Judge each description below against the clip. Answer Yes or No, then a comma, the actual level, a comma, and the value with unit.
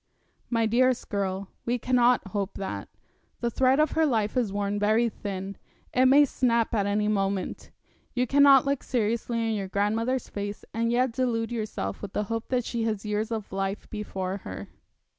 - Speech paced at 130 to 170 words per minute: No, average, 180 wpm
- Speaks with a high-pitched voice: Yes, high, 225 Hz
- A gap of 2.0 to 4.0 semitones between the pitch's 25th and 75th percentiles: Yes, average, 3.5 semitones